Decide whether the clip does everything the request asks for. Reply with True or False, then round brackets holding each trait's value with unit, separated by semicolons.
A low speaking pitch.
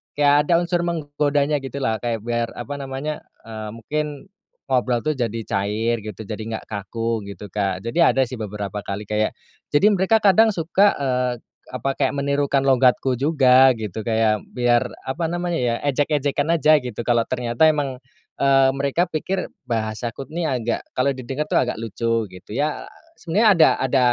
True (130 Hz)